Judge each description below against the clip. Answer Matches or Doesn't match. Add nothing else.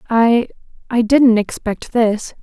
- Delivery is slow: Matches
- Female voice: Matches